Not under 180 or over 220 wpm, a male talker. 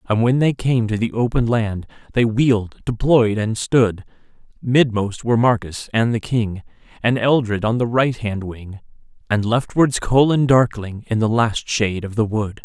No: average, 170 wpm; male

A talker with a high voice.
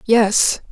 Yes: high, 220 Hz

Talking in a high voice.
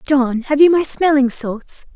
Yes: very high, 275 Hz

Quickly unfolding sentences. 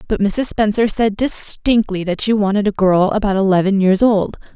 No: average, 185 wpm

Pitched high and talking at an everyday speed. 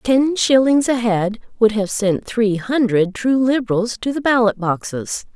Yes: high, 230 Hz; average, 170 wpm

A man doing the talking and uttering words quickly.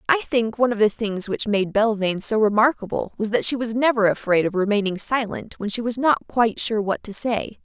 No: female; fast, 230 wpm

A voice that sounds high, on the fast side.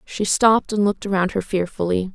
No: high, 195 Hz; average, 195 wpm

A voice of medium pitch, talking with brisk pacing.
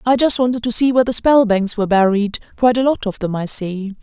No: high, 225 Hz; fast, 240 wpm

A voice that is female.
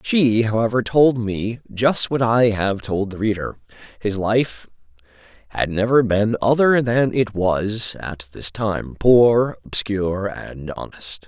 No: male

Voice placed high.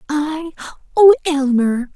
Yes: very high, 305 Hz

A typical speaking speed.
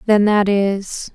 Yes: average, 155 wpm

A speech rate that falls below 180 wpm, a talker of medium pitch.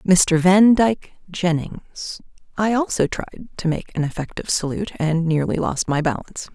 Yes: average, 140 wpm; medium, 180 Hz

